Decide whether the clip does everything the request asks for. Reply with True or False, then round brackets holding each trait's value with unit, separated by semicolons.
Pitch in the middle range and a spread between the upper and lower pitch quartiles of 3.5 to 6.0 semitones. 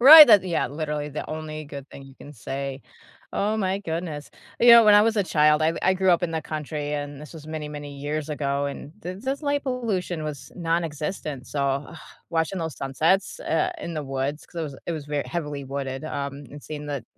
True (155 Hz; 3.8 semitones)